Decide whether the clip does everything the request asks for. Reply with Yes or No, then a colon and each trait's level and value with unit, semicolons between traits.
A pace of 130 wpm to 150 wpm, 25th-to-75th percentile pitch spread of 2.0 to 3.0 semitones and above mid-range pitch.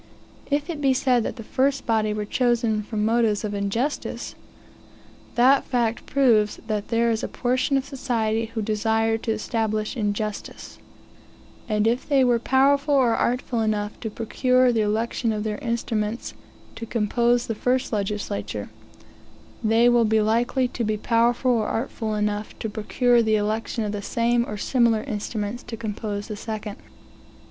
No: average, 160 wpm; narrow, 2.4 semitones; high, 225 Hz